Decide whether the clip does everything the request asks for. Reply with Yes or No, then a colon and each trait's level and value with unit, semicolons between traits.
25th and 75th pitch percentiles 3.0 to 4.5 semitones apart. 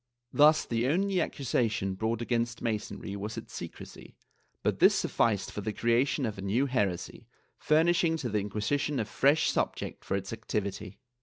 No: wide, 5.4 semitones